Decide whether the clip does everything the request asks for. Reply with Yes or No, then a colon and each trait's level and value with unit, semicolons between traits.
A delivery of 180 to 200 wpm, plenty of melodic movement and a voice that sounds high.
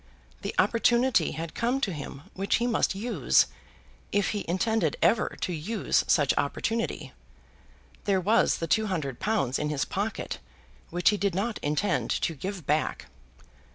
No: average, 155 wpm; wide, 5.7 semitones; high, 195 Hz